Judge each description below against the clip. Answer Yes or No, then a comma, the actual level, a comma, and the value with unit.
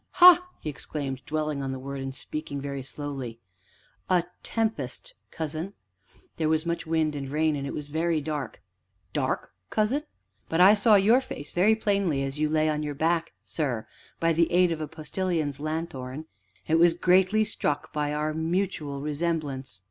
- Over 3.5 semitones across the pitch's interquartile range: No, average, 3.2 semitones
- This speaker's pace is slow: No, average, 170 wpm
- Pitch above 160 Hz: No, medium, 155 Hz